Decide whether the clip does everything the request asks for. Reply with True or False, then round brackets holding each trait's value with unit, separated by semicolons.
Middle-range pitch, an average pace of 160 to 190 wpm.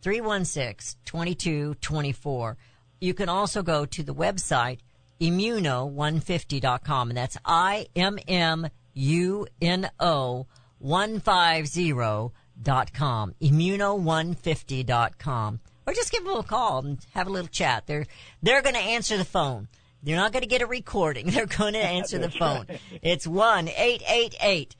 True (160 Hz; 175 wpm)